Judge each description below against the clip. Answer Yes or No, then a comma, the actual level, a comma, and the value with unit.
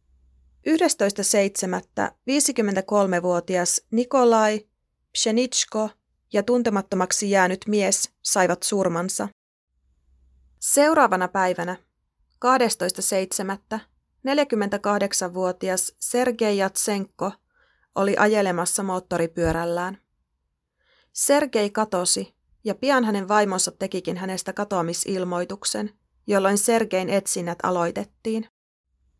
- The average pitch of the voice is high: Yes, high, 195 Hz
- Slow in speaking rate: Yes, slow, 65 wpm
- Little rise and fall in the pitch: No, average, 3.5 semitones